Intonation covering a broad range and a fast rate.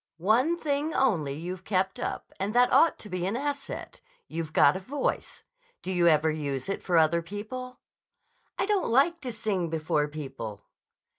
No: wide, 8.0 semitones; average, 170 wpm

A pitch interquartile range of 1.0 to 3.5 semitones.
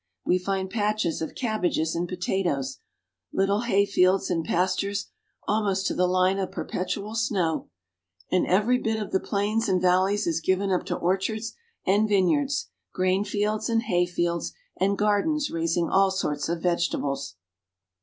Yes: average, 2.8 semitones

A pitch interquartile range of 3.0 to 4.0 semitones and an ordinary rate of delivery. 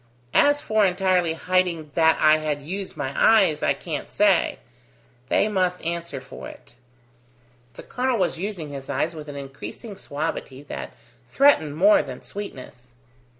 No: average, 5.1 semitones; average, 150 wpm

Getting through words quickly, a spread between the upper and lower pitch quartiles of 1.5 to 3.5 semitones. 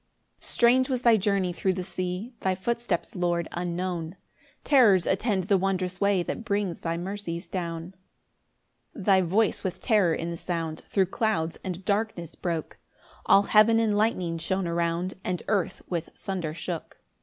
No: average, 160 wpm; average, 3.1 semitones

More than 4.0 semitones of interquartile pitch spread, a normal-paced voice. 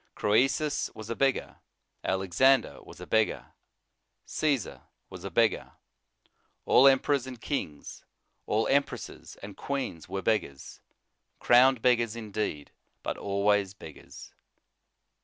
No: average, 5.1 semitones; slow, 115 wpm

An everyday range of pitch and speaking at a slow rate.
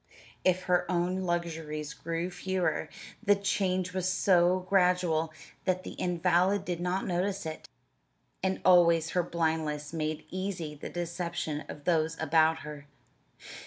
No: narrow, 2.3 semitones; slow, 130 wpm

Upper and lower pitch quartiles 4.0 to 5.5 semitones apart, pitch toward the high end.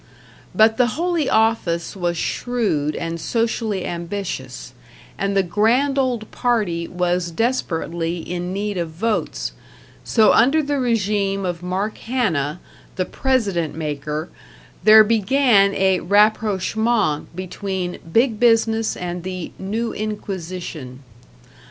Yes: average, 4.5 semitones; high, 200 Hz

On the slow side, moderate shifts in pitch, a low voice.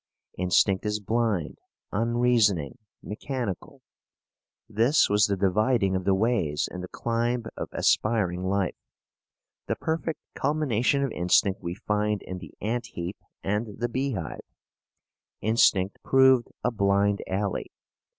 Yes: slow, 120 wpm; average, 3.9 semitones; low, 105 Hz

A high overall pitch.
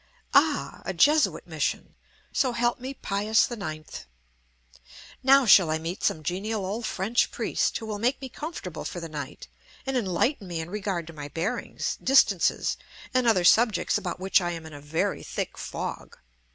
Yes: high, 200 Hz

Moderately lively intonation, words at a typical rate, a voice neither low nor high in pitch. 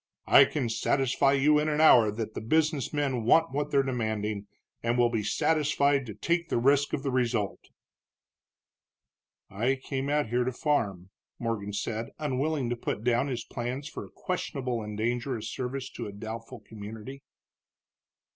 No: average, 4.1 semitones; average, 165 wpm; low, 125 Hz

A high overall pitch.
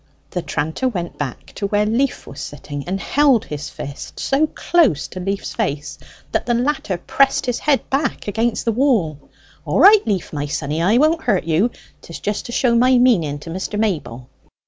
Yes: high, 205 Hz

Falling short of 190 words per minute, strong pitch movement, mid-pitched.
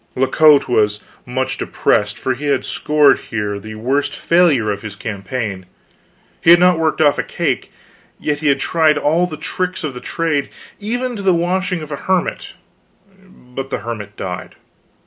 Yes: average, 175 wpm; wide, 6.8 semitones; medium, 145 Hz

